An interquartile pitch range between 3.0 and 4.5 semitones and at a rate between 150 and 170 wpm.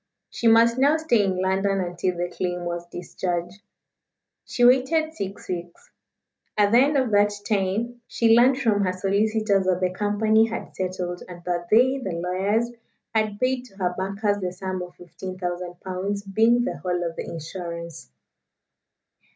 Yes: average, 4.1 semitones; average, 160 wpm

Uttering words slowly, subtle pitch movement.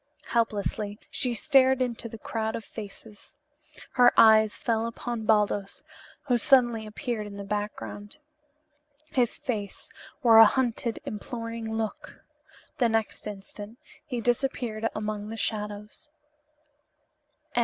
Yes: slow, 115 wpm; narrow, 2.3 semitones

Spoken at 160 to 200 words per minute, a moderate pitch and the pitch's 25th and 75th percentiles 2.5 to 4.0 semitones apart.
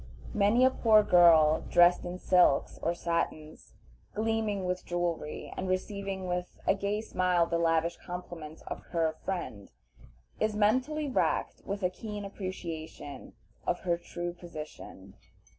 No: slow, 135 wpm; medium, 180 Hz; average, 3.1 semitones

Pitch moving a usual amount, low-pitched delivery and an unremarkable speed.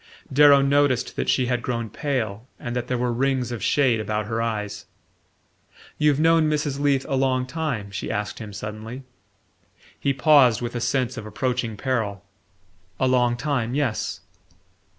Yes: average, 3.4 semitones; low, 125 Hz; average, 160 wpm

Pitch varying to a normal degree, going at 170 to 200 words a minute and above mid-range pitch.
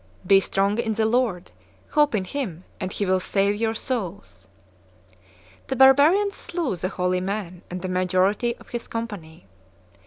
No: average, 4.6 semitones; average, 155 wpm; high, 200 Hz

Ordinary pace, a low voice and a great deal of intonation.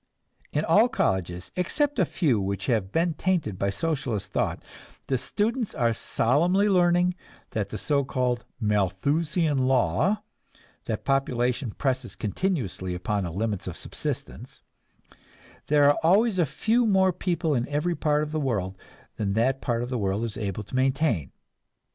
Yes: average, 150 wpm; low, 130 Hz; wide, 8.1 semitones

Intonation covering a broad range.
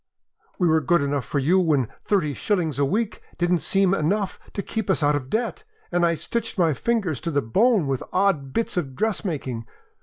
Yes: wide, 5.8 semitones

